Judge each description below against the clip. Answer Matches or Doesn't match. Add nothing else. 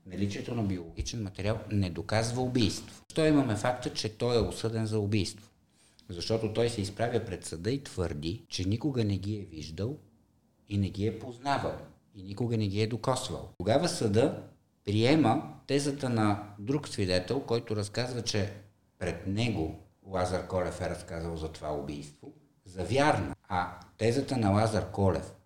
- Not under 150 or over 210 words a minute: Matches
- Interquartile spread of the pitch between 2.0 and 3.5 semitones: Doesn't match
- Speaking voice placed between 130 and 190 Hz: Doesn't match